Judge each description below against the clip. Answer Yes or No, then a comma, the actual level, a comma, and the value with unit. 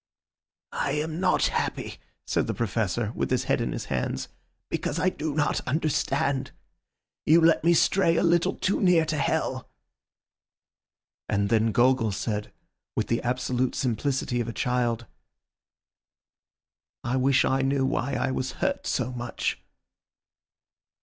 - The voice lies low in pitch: Yes, low, 130 Hz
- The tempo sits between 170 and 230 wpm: No, average, 140 wpm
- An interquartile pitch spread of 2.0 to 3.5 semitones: No, average, 4.3 semitones